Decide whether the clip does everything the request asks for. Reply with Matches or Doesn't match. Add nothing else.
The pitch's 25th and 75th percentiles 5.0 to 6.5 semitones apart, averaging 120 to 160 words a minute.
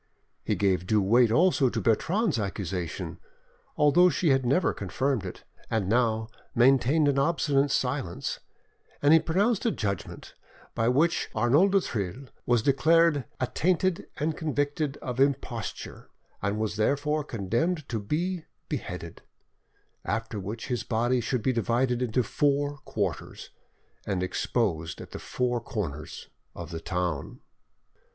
Matches